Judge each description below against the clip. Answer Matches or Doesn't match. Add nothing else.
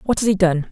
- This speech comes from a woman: Matches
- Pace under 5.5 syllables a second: Doesn't match